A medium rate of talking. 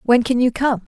No: fast, 255 wpm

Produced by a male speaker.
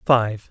Yes: male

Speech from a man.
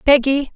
No: female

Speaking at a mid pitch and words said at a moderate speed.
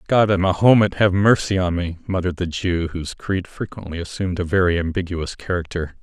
No: very low, 90 Hz; average, 180 wpm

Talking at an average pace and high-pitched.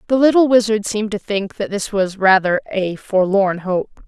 Yes: average, 190 wpm; high, 205 Hz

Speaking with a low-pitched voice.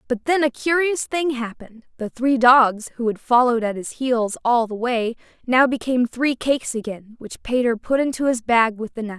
No: high, 245 Hz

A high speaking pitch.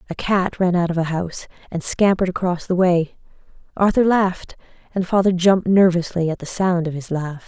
No: medium, 180 Hz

